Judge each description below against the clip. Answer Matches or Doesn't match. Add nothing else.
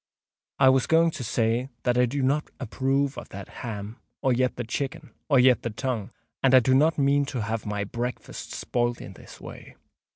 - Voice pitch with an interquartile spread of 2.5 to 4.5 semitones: Matches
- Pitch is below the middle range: Matches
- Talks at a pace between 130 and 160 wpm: Doesn't match